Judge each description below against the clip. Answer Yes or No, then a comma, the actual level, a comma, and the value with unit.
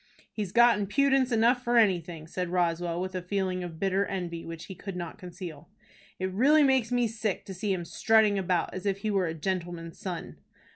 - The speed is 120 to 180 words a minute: No, average, 200 wpm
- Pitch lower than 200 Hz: Yes, high, 190 Hz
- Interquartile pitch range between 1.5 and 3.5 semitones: No, average, 3.9 semitones